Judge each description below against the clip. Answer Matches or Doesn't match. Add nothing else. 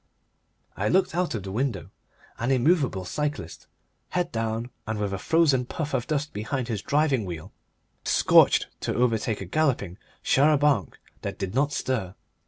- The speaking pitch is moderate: Doesn't match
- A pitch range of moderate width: Doesn't match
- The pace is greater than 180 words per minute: Doesn't match